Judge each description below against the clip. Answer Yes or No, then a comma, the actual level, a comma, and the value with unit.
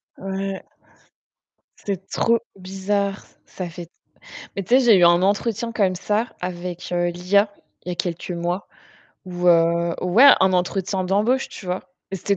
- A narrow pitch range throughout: Yes, narrow, 2.2 semitones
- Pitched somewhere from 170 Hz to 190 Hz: Yes, medium, 185 Hz